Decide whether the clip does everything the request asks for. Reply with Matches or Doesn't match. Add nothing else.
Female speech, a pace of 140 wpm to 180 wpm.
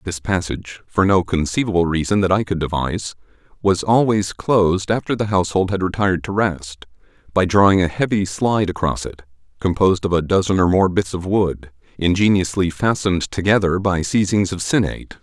Doesn't match